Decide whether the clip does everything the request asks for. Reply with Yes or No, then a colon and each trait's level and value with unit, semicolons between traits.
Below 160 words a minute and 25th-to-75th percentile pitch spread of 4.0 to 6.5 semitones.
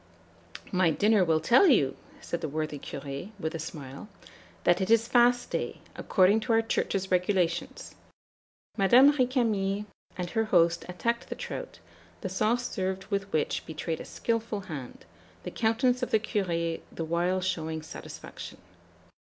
Yes: average, 150 wpm; average, 5.2 semitones